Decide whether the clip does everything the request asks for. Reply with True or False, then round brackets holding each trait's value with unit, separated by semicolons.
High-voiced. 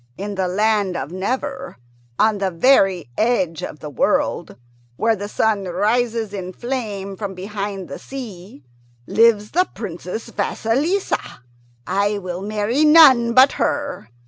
True (210 Hz)